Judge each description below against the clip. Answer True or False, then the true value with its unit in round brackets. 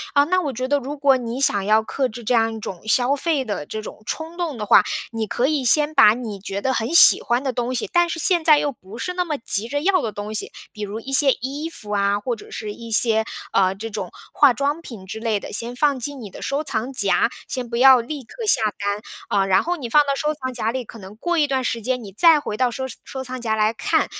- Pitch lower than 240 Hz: False (245 Hz)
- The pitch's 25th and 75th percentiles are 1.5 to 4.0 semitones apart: False (4.8 semitones)